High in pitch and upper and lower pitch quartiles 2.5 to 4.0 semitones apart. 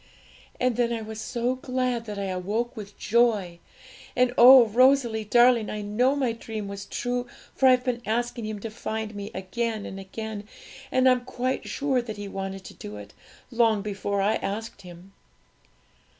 Yes: high, 225 Hz; average, 3.3 semitones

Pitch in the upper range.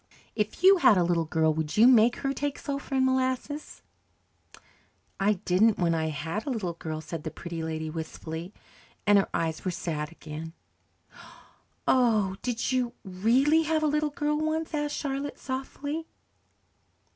Yes: high, 215 Hz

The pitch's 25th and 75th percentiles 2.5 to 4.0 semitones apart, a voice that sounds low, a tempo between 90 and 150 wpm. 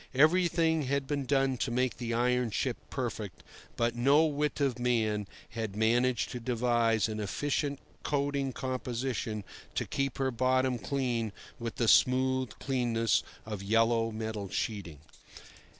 Yes: average, 2.9 semitones; low, 125 Hz; slow, 135 wpm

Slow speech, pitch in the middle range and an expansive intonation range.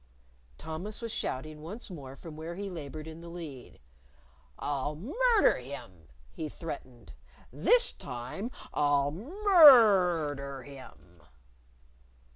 Yes: slow, 115 wpm; medium, 160 Hz; wide, 6.6 semitones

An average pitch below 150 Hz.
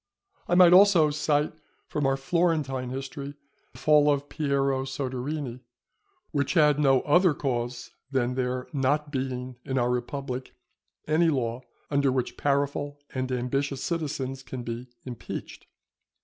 Yes: low, 135 Hz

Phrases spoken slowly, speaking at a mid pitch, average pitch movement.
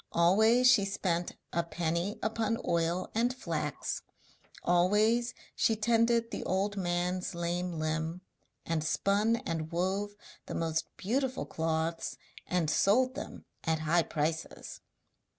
Yes: slow, 120 wpm; medium, 180 Hz; average, 4.7 semitones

